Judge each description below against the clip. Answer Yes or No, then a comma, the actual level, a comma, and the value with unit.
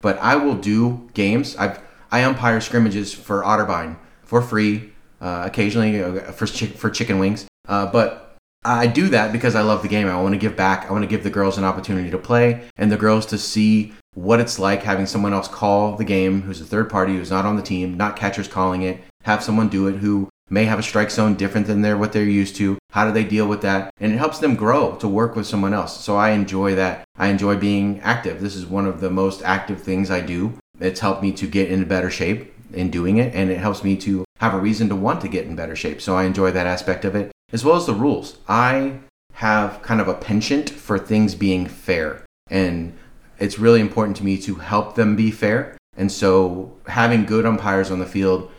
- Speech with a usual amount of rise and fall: No, narrow, 2.1 semitones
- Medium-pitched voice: No, low, 100 Hz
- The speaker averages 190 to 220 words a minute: No, fast, 235 wpm